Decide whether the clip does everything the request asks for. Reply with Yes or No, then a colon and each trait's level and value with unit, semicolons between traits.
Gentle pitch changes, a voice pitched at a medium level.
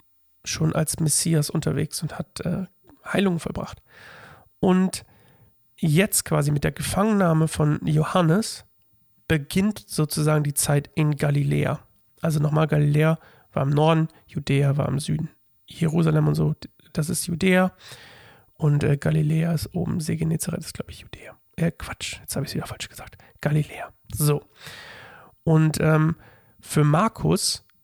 Yes: narrow, 2.3 semitones; medium, 155 Hz